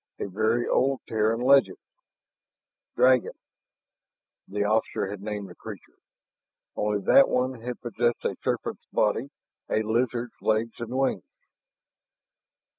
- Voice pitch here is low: Yes, low, 115 Hz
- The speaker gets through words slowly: Yes, slow, 115 wpm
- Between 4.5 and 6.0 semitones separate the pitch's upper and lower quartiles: No, average, 2.8 semitones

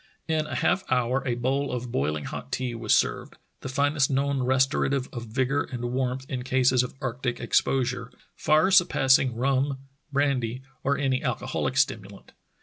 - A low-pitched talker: Yes, low, 130 Hz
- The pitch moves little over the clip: Yes, narrow, 1.9 semitones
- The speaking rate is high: No, average, 165 wpm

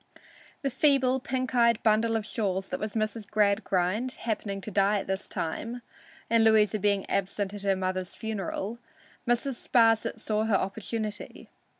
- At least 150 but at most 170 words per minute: Yes, average, 155 wpm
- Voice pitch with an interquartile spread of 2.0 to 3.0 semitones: Yes, narrow, 2.6 semitones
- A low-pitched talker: No, high, 215 Hz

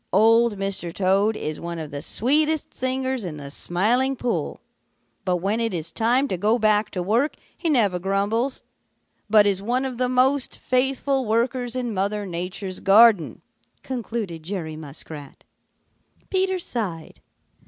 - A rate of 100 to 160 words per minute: Yes, average, 145 wpm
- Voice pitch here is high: Yes, high, 215 Hz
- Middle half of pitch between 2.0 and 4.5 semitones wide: No, wide, 5.6 semitones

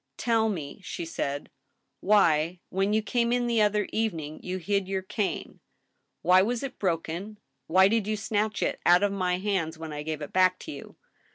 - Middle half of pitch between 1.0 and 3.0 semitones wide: No, average, 4.1 semitones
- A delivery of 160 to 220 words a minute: Yes, average, 200 wpm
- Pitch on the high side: Yes, high, 195 Hz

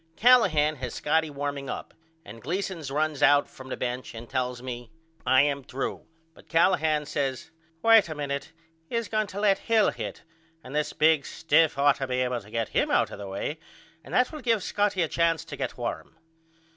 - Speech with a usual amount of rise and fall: Yes, average, 4.5 semitones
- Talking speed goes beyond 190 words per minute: Yes, average, 200 wpm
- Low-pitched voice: No, medium, 145 Hz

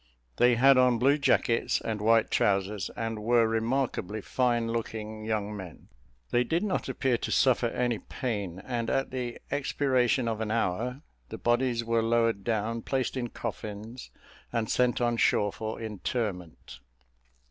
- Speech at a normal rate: Yes, average, 150 wpm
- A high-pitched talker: No, low, 115 Hz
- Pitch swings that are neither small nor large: No, narrow, 2.3 semitones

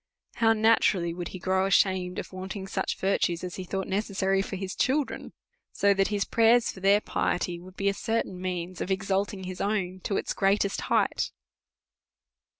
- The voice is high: Yes, high, 195 Hz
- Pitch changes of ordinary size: No, narrow, 1.5 semitones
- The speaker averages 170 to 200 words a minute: Yes, average, 175 wpm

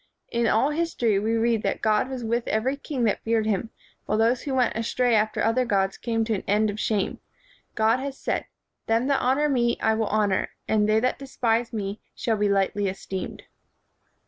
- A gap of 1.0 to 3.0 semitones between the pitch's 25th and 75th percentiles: Yes, narrow, 2.6 semitones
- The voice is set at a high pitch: Yes, high, 225 Hz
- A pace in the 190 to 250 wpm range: Yes, average, 200 wpm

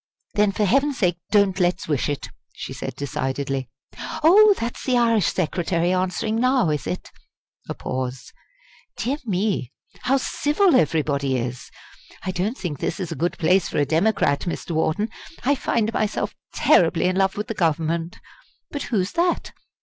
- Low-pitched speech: No, medium, 185 Hz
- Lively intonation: Yes, wide, 6.3 semitones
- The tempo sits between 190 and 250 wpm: No, average, 160 wpm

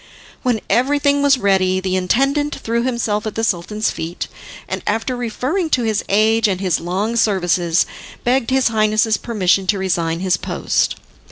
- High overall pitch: Yes, high, 215 Hz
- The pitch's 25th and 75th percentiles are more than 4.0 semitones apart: Yes, average, 4.6 semitones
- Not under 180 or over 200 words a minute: No, average, 160 wpm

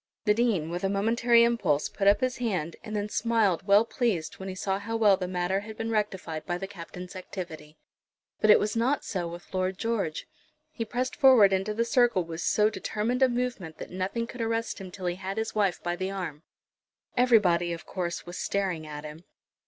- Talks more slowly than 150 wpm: No, fast, 205 wpm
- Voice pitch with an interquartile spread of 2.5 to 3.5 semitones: No, average, 4.3 semitones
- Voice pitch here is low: No, high, 195 Hz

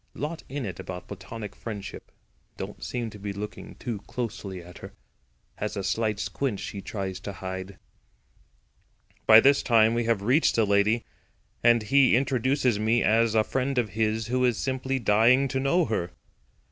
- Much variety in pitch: No, average, 3.9 semitones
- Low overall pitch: Yes, low, 115 Hz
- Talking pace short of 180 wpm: Yes, average, 170 wpm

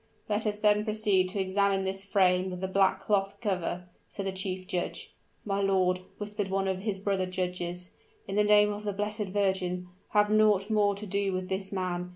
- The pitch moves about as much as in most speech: No, narrow, 1.9 semitones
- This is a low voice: No, high, 195 Hz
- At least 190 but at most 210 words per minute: Yes, average, 195 wpm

